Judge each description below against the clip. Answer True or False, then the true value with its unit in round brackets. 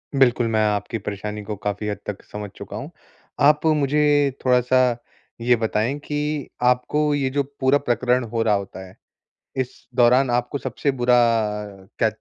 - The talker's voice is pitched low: True (125 Hz)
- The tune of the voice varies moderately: True (4.2 semitones)